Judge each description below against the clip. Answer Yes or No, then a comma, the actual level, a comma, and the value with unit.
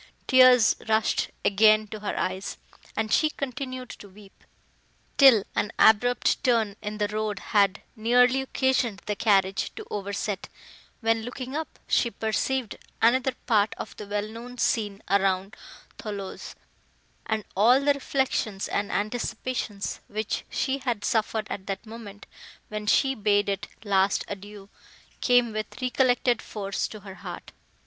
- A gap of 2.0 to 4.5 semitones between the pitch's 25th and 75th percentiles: Yes, average, 3.4 semitones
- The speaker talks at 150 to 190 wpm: No, average, 140 wpm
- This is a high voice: Yes, high, 215 Hz